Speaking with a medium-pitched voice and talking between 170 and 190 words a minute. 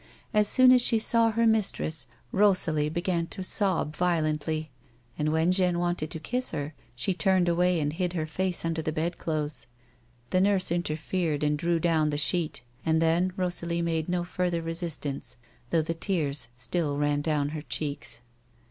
Yes: medium, 170 Hz; average, 175 wpm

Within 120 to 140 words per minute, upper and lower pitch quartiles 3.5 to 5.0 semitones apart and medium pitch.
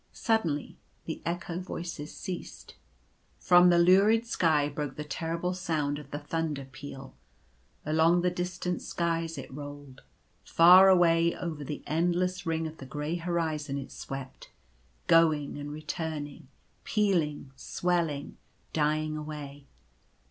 No: slow, 135 wpm; average, 3.1 semitones; medium, 160 Hz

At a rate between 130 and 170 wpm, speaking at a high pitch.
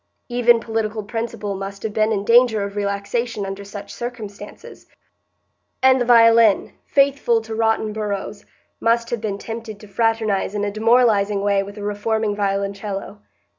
Yes: average, 150 wpm; high, 215 Hz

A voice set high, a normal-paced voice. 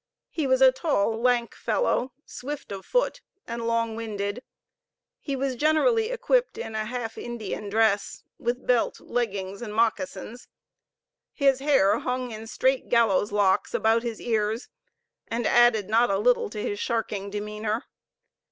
Yes: high, 230 Hz; average, 145 wpm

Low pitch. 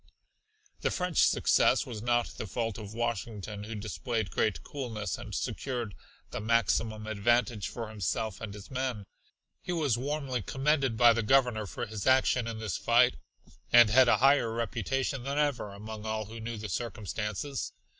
Yes: low, 115 Hz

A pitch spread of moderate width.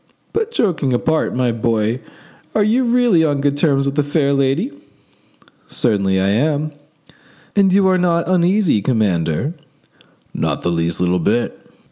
No: wide, 8.4 semitones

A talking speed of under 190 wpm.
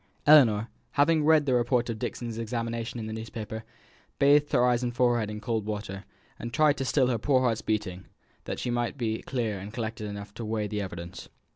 No: fast, 205 wpm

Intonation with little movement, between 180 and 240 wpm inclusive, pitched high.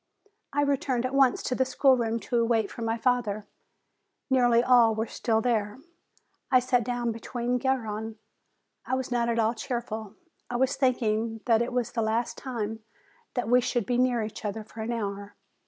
Yes: narrow, 2.1 semitones; average, 190 wpm; high, 235 Hz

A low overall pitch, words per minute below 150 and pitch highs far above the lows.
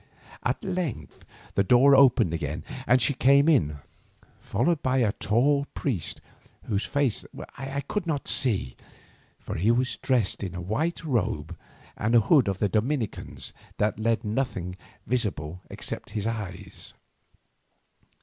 Yes: low, 115 Hz; slow, 135 wpm; wide, 5.8 semitones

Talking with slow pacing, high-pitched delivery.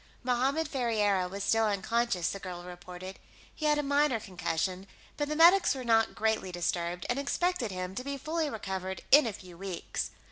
No: average, 180 wpm; high, 220 Hz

